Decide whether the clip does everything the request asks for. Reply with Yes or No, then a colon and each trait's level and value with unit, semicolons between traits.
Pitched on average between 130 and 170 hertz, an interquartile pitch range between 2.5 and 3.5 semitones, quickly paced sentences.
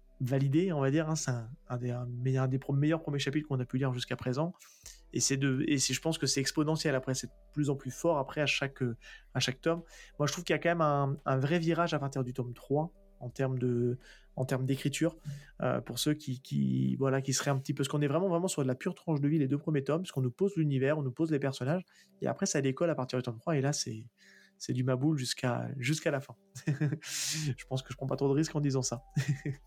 Yes: medium, 140 Hz; average, 3.1 semitones; fast, 275 wpm